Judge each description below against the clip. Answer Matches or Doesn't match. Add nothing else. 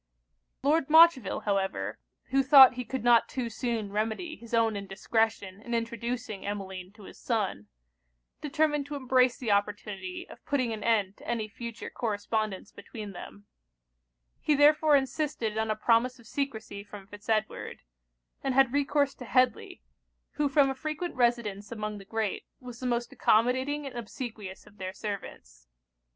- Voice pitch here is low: Doesn't match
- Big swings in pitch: Doesn't match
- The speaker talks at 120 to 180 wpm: Matches